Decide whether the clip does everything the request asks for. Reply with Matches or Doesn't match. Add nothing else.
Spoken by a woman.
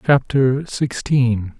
Doesn't match